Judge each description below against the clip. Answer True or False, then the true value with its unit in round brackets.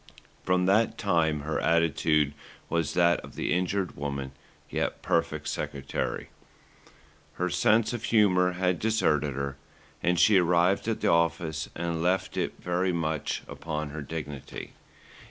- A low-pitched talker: True (85 Hz)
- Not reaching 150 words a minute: True (135 wpm)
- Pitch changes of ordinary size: True (3.1 semitones)